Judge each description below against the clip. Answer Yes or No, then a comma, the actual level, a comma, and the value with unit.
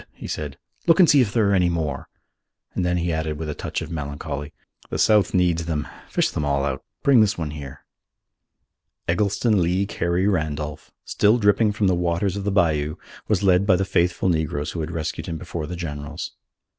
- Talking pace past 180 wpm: Yes, average, 200 wpm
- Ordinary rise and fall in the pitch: Yes, average, 4.3 semitones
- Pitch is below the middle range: Yes, very low, 85 Hz